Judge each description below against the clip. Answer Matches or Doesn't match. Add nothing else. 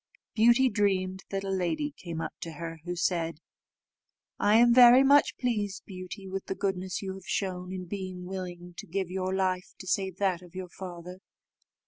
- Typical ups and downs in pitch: Doesn't match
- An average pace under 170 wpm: Doesn't match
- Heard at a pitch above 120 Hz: Matches